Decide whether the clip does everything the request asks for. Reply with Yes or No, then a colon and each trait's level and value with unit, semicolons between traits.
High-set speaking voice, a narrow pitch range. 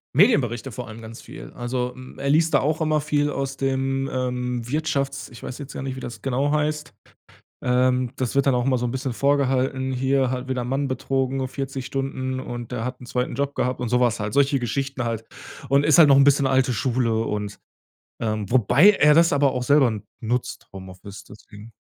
No: low, 130 Hz; narrow, 2.0 semitones